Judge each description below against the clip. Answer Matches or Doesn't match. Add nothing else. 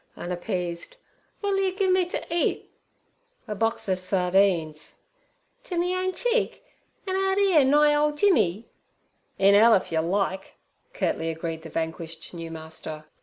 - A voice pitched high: Matches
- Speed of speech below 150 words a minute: Matches